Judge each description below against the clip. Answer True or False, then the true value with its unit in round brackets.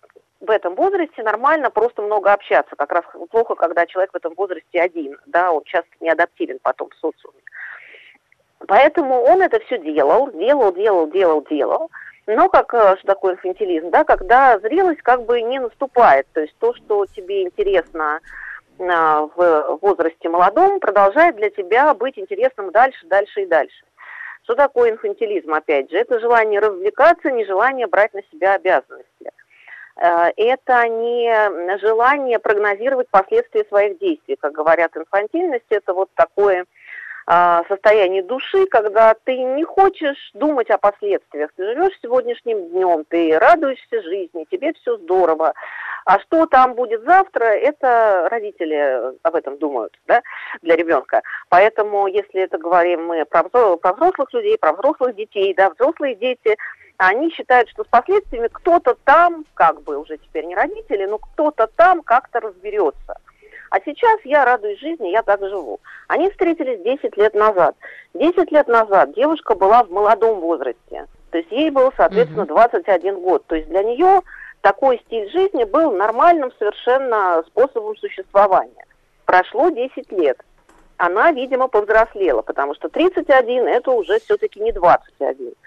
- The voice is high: True (245 Hz)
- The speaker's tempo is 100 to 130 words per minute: False (145 wpm)